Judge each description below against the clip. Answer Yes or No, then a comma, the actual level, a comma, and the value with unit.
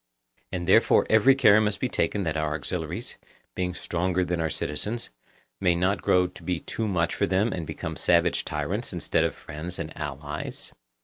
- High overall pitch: No, very low, 90 Hz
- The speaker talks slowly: No, average, 180 wpm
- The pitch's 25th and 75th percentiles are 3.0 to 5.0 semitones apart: Yes, average, 4.0 semitones